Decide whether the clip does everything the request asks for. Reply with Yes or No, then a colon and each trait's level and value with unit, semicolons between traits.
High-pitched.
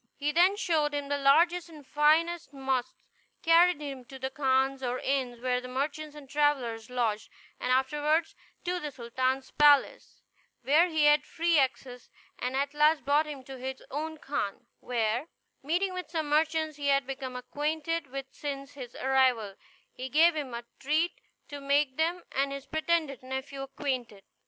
Yes: very high, 280 Hz